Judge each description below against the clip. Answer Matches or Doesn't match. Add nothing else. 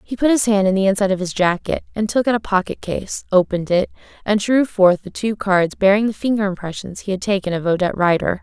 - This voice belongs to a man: Doesn't match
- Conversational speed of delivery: Doesn't match